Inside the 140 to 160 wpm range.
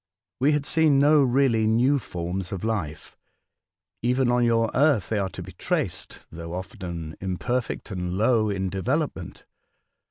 Yes: average, 150 wpm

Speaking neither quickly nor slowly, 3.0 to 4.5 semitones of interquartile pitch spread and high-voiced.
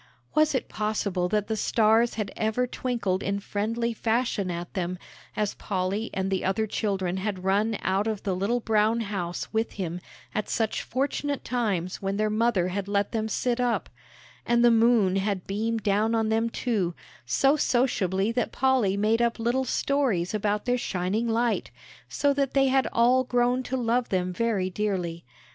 Yes: average, 175 wpm; average, 3.5 semitones; high, 215 Hz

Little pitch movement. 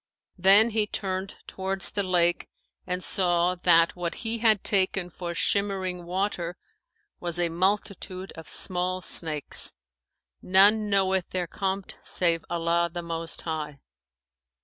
Yes: narrow, 2.1 semitones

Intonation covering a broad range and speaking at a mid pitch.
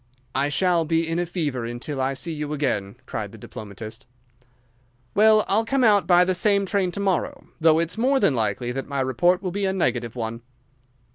Yes: wide, 6.6 semitones; medium, 165 Hz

